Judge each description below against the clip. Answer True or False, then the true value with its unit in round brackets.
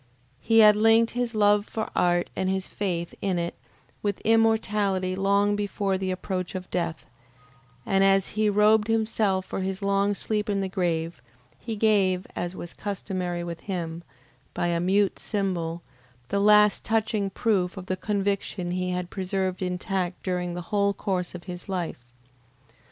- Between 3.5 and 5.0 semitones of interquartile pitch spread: False (2.5 semitones)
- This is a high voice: True (195 Hz)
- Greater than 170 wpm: False (160 wpm)